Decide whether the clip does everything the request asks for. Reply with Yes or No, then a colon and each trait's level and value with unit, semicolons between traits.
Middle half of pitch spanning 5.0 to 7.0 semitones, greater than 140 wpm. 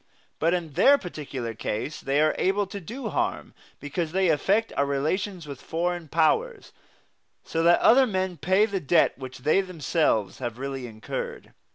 Yes: average, 5.3 semitones; average, 165 wpm